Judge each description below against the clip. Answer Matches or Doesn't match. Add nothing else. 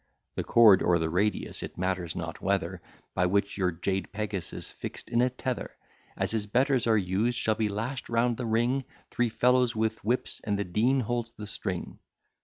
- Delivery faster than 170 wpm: Matches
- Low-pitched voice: Matches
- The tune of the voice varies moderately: Matches